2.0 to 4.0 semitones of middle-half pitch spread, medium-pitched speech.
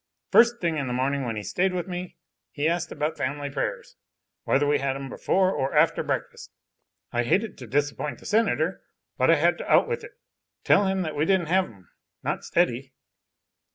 No: average, 5.3 semitones; medium, 150 Hz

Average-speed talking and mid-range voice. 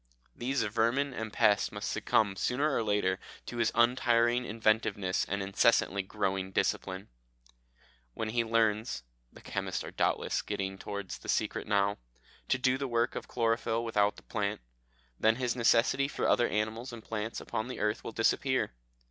No: average, 160 wpm; low, 110 Hz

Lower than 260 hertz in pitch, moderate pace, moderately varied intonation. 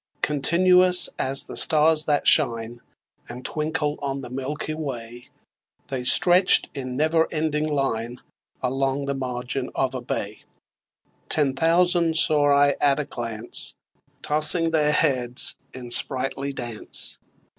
No: medium, 140 Hz; slow, 125 wpm; average, 3.5 semitones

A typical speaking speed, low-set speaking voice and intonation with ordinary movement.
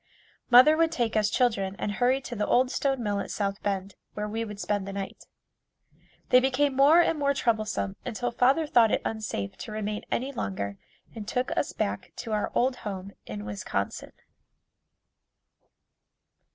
No: average, 165 wpm; high, 220 Hz; average, 4.2 semitones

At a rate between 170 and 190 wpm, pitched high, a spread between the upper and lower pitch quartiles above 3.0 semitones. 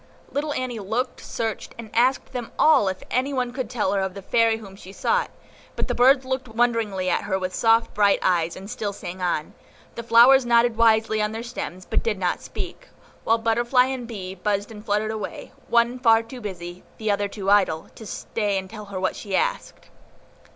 No: fast, 205 wpm; high, 220 Hz; average, 3.5 semitones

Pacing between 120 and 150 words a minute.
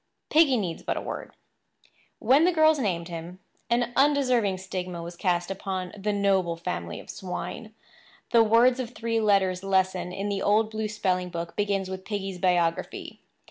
No: average, 165 wpm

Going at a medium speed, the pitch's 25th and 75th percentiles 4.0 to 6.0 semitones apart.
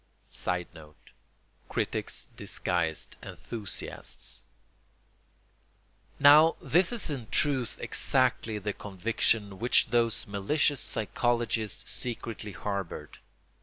No: slow, 80 wpm; average, 4.5 semitones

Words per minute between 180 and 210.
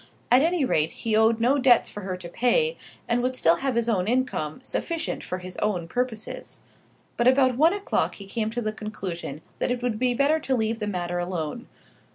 Yes: fast, 205 wpm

